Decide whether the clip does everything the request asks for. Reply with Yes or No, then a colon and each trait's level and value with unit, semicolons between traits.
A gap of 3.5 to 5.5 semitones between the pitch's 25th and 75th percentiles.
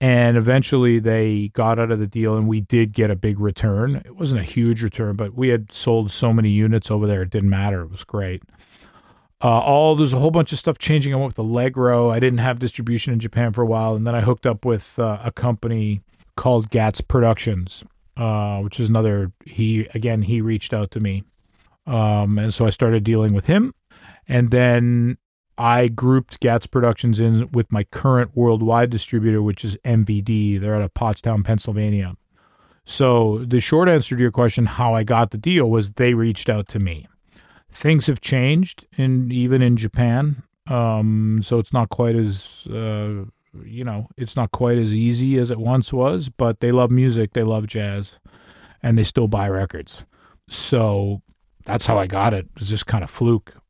No: narrow, 2.6 semitones